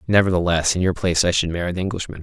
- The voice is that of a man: Yes, male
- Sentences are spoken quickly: Yes, fast, 240 wpm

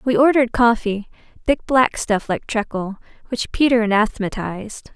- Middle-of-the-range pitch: No, high, 225 Hz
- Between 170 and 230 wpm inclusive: No, slow, 135 wpm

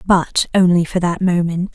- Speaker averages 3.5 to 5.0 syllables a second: Yes, 4.5 syllables/s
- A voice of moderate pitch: Yes, medium, 175 Hz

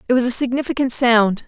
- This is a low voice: No, very high, 250 Hz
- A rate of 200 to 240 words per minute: Yes, fast, 205 wpm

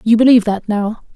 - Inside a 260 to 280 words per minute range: No, fast, 205 wpm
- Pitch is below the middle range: No, high, 220 Hz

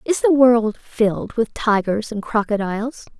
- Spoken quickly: No, average, 150 wpm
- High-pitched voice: Yes, high, 225 Hz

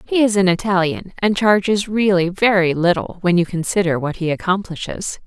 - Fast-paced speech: No, average, 170 wpm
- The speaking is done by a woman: Yes, female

